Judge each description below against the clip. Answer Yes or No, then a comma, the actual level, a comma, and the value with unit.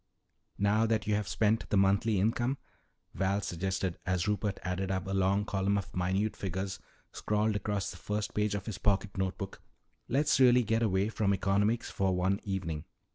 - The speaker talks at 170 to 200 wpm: Yes, average, 180 wpm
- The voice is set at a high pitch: No, low, 100 Hz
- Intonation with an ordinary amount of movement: No, narrow, 2.0 semitones